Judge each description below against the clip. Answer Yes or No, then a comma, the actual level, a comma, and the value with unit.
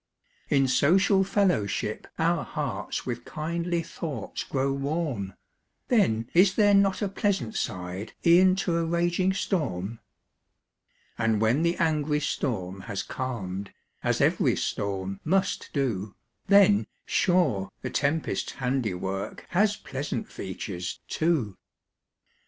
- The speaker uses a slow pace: Yes, slow, 115 wpm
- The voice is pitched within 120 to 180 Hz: Yes, medium, 140 Hz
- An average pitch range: No, wide, 8.8 semitones